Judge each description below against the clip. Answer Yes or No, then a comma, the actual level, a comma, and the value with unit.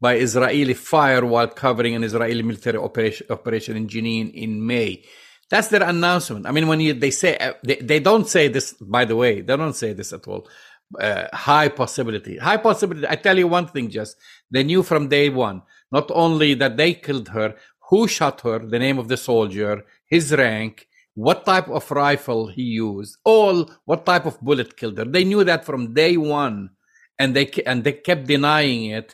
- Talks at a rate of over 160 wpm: Yes, average, 195 wpm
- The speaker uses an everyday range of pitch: No, wide, 5.8 semitones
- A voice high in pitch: No, low, 135 Hz